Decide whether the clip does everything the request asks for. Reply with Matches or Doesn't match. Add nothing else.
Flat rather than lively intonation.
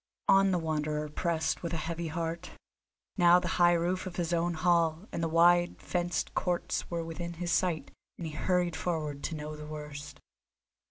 Matches